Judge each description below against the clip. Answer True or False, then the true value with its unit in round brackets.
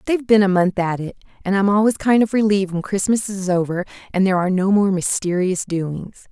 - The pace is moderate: False (220 wpm)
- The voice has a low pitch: False (195 Hz)